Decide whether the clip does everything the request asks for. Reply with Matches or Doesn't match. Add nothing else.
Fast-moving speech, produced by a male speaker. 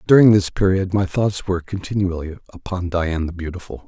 Doesn't match